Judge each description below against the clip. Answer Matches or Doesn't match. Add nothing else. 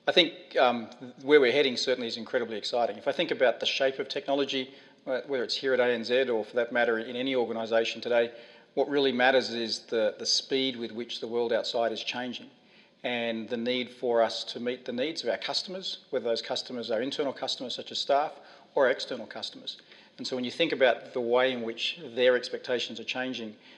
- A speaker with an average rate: Doesn't match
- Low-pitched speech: Matches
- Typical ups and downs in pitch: Doesn't match